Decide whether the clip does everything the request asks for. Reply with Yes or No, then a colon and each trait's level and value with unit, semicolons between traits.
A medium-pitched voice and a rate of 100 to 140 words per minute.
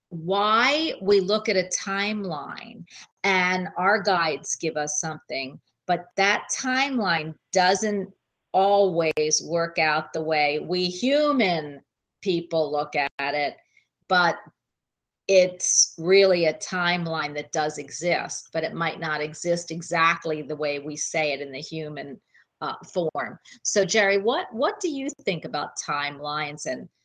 Yes: medium, 170 Hz; slow, 135 wpm